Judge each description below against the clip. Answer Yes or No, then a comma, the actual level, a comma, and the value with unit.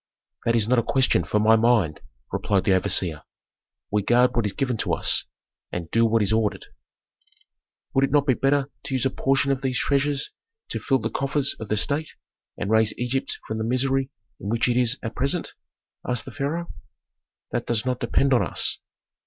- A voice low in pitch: Yes, low, 125 Hz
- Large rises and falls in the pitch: No, average, 3.5 semitones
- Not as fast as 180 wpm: No, average, 195 wpm